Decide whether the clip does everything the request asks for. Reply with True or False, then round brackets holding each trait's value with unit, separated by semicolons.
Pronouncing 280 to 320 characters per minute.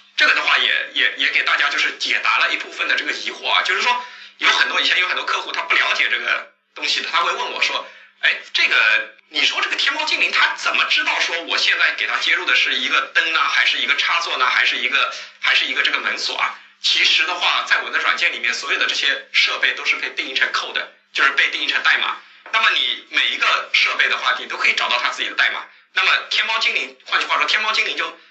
False (370 characters per minute)